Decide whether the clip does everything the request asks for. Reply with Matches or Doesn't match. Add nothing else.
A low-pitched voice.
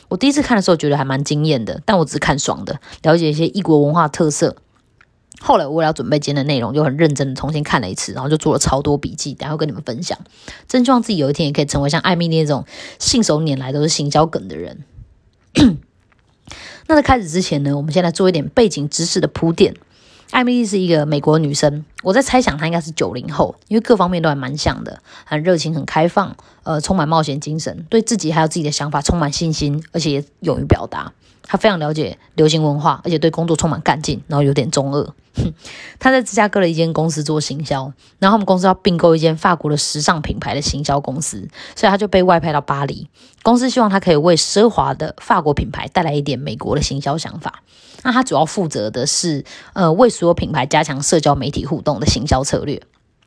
Doesn't match